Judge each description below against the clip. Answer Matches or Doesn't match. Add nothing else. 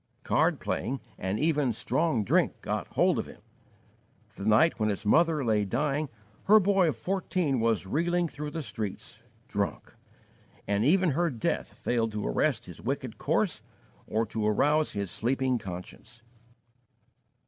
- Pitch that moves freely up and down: Matches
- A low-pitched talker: Matches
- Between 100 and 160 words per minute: Matches